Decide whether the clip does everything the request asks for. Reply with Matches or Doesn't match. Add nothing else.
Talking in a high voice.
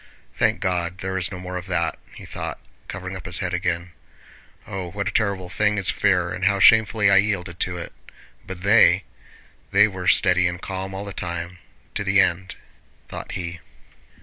Doesn't match